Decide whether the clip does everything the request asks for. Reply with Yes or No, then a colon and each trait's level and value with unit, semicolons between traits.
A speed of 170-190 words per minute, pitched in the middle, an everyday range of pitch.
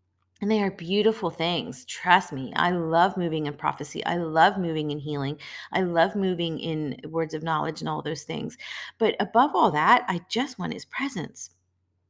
Yes: average, 185 wpm; medium, 165 Hz; average, 3.2 semitones